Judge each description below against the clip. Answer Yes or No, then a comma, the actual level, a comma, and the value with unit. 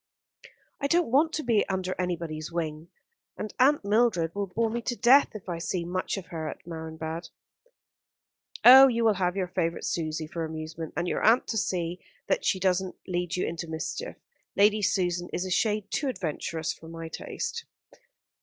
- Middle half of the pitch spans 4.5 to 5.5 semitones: Yes, average, 4.9 semitones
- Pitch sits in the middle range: Yes, medium, 180 Hz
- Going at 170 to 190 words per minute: Yes, average, 180 wpm